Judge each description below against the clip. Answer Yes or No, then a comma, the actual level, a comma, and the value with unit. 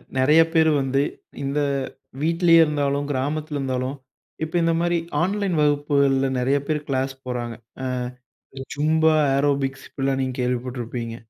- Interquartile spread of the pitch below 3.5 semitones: Yes, average, 2.9 semitones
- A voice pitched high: No, medium, 140 Hz